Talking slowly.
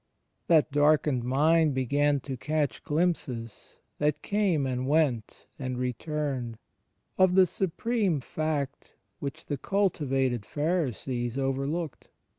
Yes: slow, 105 wpm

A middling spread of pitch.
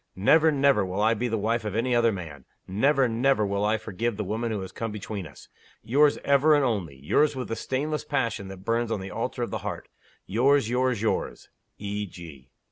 Yes: average, 4.5 semitones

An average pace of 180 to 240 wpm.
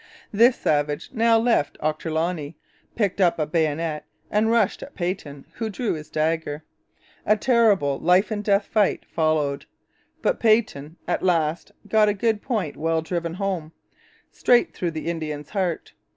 No: average, 150 wpm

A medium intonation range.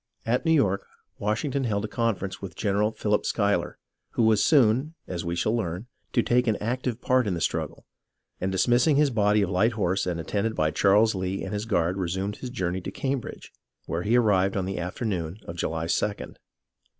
Yes: average, 3.9 semitones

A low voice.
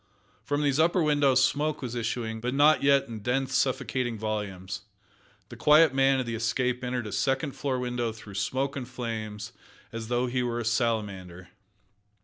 Yes: low, 125 Hz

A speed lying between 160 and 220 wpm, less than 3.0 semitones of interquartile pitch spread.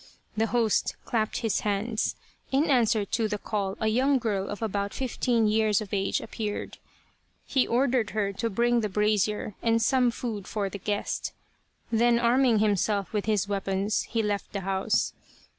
Yes: average, 165 wpm; narrow, 2.5 semitones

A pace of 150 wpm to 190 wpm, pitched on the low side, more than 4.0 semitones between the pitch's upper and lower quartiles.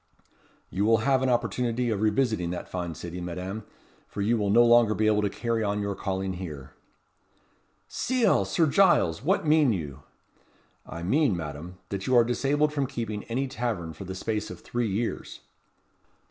Yes: average, 175 wpm; low, 110 Hz; average, 4.8 semitones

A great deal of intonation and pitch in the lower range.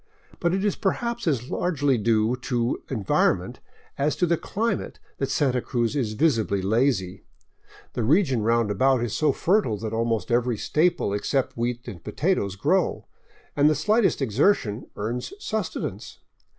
Yes: wide, 5.9 semitones; low, 125 Hz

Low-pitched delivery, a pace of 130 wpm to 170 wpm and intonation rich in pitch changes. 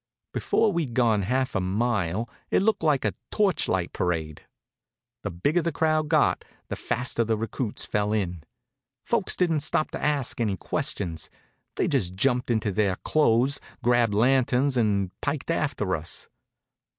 Yes: low, 120 Hz; average, 150 wpm; wide, 6.2 semitones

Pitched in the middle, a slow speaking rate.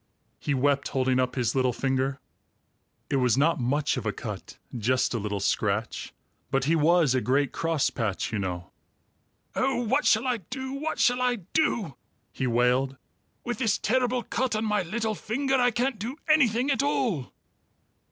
No: medium, 165 Hz; average, 170 wpm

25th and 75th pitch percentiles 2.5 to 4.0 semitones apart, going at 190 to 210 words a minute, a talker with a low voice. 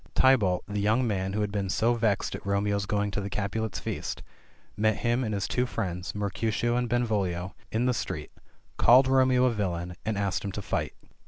Yes: average, 3.1 semitones; average, 195 wpm; low, 105 Hz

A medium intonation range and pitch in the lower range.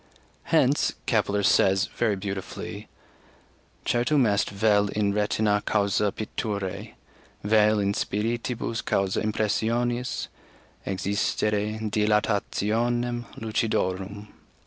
No: narrow, 1.9 semitones; low, 105 Hz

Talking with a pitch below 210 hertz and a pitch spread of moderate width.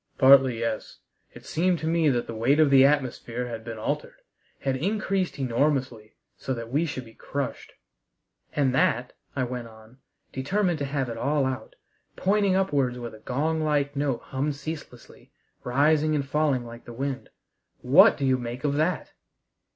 Yes: low, 135 Hz; average, 3.6 semitones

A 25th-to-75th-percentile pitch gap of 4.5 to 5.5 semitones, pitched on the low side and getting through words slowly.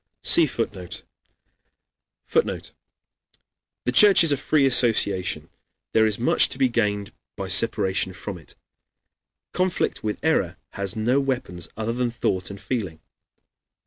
Yes: average, 4.9 semitones; low, 110 Hz; slow, 130 wpm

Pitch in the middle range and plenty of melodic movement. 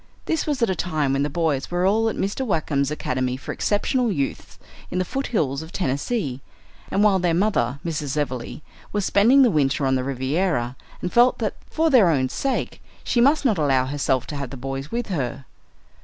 Yes: medium, 160 Hz; wide, 7.7 semitones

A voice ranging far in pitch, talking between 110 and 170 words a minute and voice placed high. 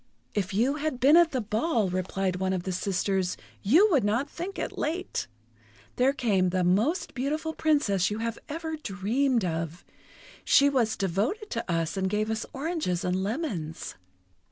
Yes: wide, 7.4 semitones; average, 165 wpm; high, 220 Hz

